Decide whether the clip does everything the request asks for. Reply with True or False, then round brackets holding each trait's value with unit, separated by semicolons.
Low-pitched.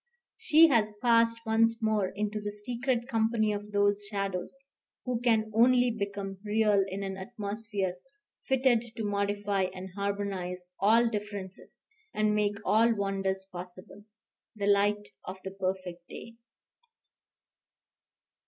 False (205 Hz)